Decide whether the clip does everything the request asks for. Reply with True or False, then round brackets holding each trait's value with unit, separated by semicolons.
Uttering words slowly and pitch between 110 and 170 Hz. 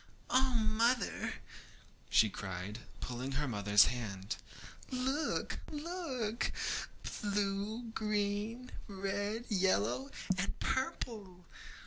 False (85 wpm; 205 Hz)